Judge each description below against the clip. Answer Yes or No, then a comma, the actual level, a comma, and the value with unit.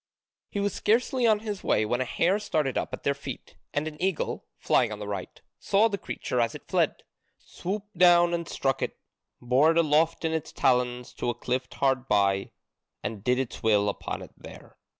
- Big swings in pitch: Yes, wide, 6.7 semitones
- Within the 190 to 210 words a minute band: Yes, average, 200 wpm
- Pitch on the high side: No, medium, 140 Hz